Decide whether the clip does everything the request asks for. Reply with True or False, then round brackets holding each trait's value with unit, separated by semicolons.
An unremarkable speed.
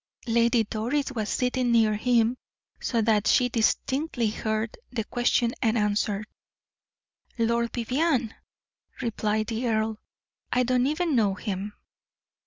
False (125 wpm)